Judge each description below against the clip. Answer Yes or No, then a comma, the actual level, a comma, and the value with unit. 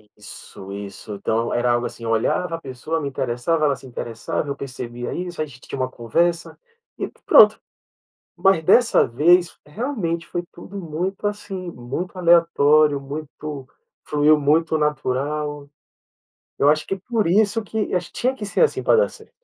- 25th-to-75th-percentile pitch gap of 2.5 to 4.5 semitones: No, wide, 5.6 semitones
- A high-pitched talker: No, medium, 155 Hz